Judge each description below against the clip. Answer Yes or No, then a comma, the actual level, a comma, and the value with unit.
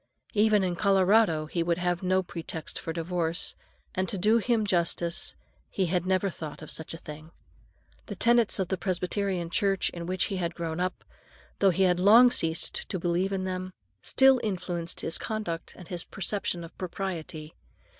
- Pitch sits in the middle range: Yes, medium, 180 Hz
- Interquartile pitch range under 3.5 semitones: Yes, narrow, 2.5 semitones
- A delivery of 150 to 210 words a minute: Yes, average, 180 wpm